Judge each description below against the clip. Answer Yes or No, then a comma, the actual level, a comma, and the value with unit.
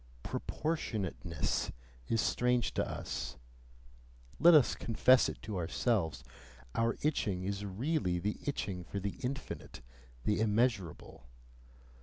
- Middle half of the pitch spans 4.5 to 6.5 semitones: Yes, average, 4.9 semitones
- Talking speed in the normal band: No, slow, 110 wpm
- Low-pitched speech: Yes, low, 105 Hz